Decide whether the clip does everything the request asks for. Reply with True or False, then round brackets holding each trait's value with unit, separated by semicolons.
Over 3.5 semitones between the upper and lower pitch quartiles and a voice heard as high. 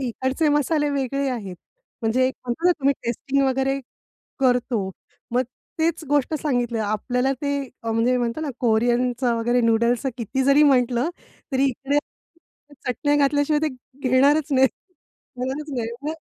False (2.9 semitones; 260 Hz)